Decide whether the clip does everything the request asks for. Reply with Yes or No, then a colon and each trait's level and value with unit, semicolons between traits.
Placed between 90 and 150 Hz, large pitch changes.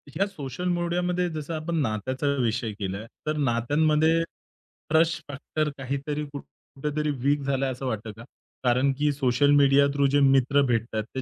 No: medium, 140 Hz; average, 3.2 semitones